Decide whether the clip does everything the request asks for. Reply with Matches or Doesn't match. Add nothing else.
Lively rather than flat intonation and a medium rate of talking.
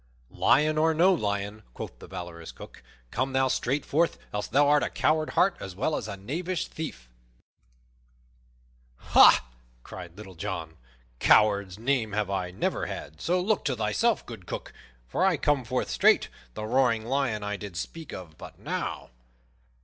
Matches